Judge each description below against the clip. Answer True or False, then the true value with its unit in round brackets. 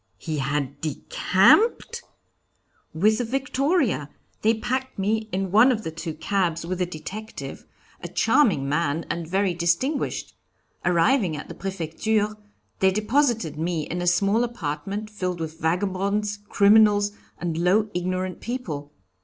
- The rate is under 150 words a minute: True (135 wpm)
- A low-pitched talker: False (190 Hz)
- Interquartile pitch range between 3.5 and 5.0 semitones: True (4.7 semitones)